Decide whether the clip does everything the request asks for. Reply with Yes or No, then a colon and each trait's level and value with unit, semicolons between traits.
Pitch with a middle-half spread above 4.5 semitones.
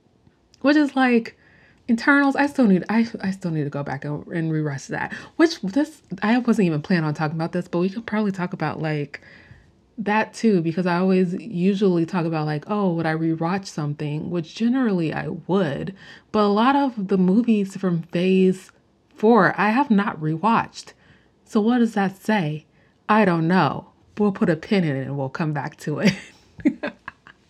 Yes: average, 5.1 semitones